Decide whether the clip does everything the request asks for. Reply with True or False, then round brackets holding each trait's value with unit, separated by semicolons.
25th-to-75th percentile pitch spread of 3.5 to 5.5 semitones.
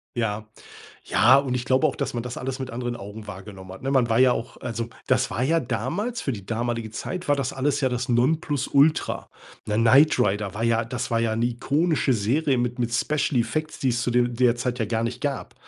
False (2.9 semitones)